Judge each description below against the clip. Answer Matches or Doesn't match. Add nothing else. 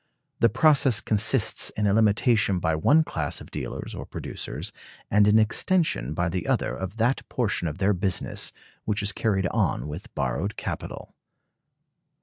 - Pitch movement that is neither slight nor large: Matches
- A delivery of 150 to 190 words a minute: Matches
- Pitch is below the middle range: Matches